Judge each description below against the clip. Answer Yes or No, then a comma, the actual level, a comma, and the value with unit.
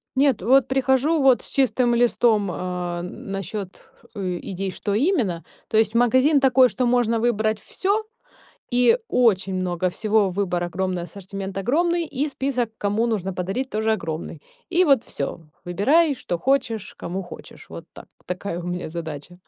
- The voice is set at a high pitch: Yes, high, 215 Hz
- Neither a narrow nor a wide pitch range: No, wide, 6.0 semitones